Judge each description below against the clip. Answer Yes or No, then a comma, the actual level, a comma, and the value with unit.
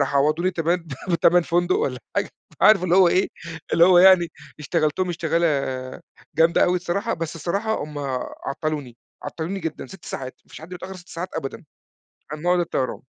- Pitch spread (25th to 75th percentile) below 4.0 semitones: Yes, average, 2.9 semitones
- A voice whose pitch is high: No, medium, 170 Hz